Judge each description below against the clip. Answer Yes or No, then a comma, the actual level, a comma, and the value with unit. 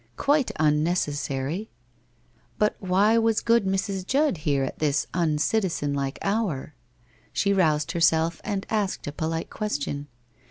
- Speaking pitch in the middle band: Yes, medium, 175 Hz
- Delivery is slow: Yes, slow, 125 wpm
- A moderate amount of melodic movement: No, wide, 5.8 semitones